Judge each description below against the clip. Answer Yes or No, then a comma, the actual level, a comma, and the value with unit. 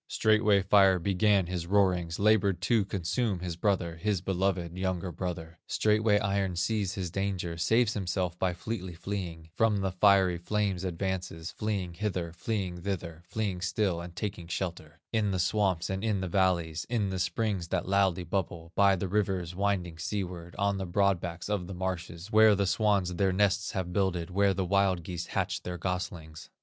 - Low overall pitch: Yes, very low, 95 Hz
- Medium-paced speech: Yes, average, 175 wpm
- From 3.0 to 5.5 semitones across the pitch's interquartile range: No, narrow, 2.4 semitones